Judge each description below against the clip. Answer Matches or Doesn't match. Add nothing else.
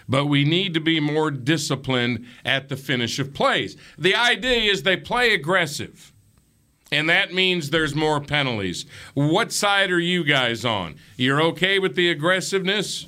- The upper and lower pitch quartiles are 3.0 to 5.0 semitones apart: Doesn't match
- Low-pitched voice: Doesn't match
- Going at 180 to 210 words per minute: Doesn't match